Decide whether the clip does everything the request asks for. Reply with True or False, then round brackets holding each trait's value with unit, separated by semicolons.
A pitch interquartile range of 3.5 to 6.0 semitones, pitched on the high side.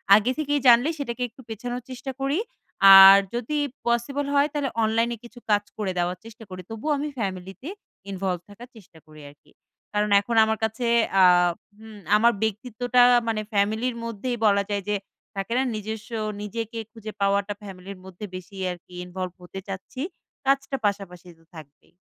True (3.8 semitones; 220 Hz)